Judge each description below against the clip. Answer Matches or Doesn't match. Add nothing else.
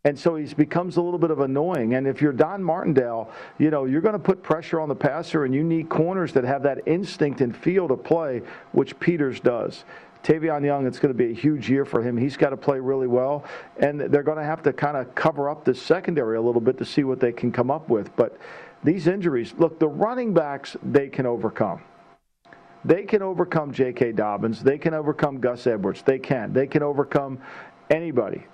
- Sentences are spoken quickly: Matches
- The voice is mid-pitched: Matches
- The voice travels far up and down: Doesn't match